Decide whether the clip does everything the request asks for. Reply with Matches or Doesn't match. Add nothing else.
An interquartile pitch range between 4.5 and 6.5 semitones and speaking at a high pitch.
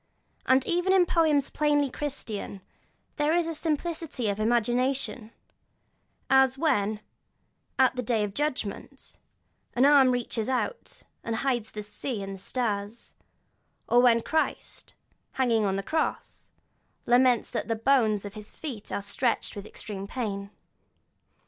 Matches